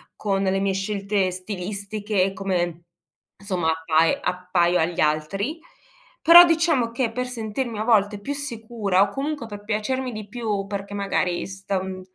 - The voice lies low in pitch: No, high, 200 Hz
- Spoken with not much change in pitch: No, average, 3.5 semitones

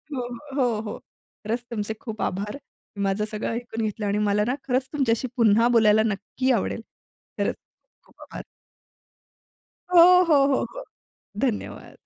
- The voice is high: Yes, high, 225 Hz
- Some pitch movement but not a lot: Yes, average, 3.3 semitones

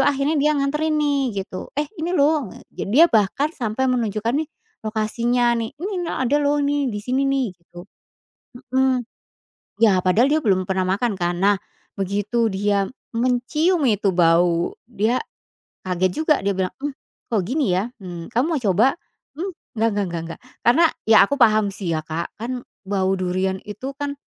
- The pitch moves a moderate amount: No, wide, 6.6 semitones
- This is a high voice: Yes, high, 230 Hz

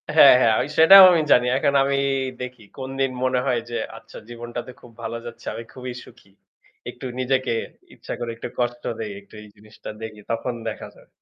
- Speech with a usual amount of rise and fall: No, narrow, 2.2 semitones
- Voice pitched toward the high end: No, low, 120 Hz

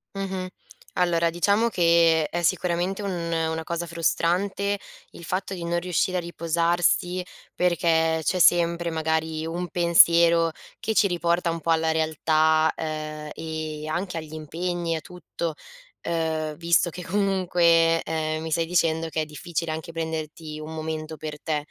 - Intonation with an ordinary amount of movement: No, narrow, 1.5 semitones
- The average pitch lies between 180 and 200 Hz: No, medium, 165 Hz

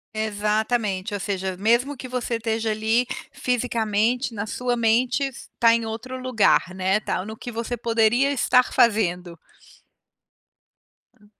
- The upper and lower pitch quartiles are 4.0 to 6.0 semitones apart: No, average, 2.7 semitones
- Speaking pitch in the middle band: No, high, 225 Hz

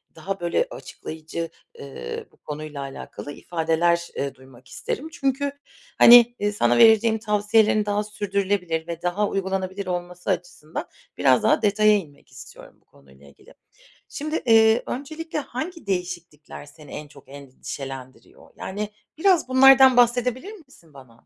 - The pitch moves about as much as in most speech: No, wide, 7.1 semitones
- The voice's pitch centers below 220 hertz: Yes, high, 190 Hz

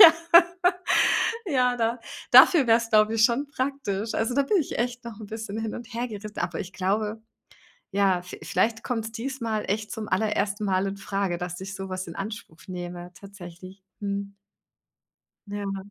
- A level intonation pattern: No, average, 3.1 semitones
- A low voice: No, high, 210 Hz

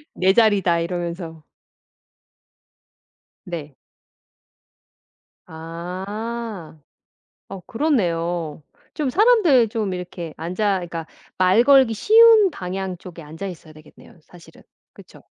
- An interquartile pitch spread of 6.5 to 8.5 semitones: No, average, 5.1 semitones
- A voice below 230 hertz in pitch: Yes, medium, 185 Hz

